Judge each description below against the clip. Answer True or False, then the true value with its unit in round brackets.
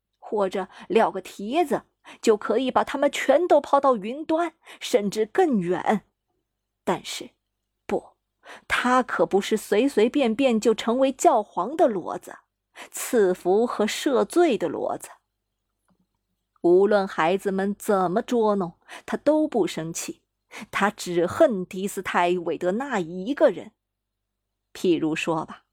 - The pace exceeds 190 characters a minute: False (185 characters per minute)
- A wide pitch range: True (6.5 semitones)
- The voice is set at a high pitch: True (210 Hz)